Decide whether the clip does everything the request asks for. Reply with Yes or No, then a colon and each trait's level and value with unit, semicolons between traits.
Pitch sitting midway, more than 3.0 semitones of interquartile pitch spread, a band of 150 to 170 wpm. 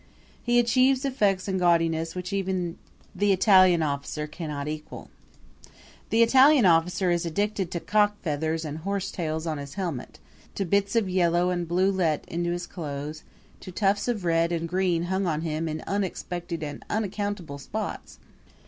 Yes: medium, 175 Hz; average, 3.5 semitones; average, 155 wpm